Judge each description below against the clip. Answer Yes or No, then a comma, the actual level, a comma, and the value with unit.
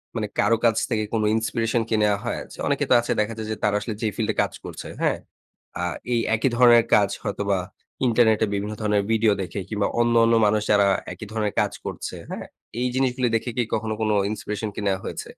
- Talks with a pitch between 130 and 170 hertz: No, low, 110 Hz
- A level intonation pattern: Yes, narrow, 1.7 semitones